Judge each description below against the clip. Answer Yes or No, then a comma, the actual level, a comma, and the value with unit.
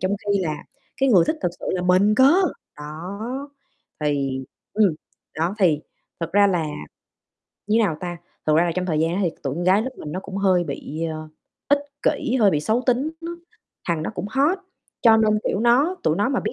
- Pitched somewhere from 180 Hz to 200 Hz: Yes, high, 190 Hz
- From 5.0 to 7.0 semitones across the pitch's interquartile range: Yes, wide, 5.5 semitones